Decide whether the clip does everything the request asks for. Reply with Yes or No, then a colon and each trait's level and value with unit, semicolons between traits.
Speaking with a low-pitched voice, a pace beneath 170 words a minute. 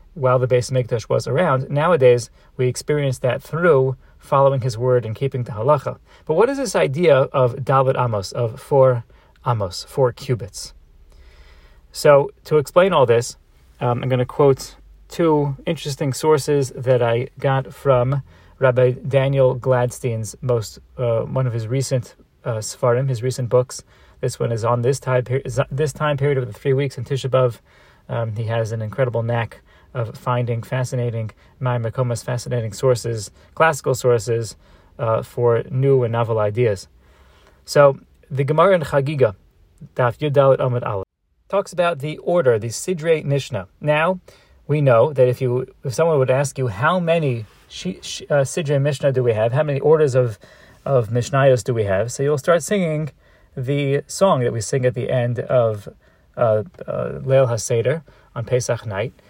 Yes: low, 130 Hz; average, 160 wpm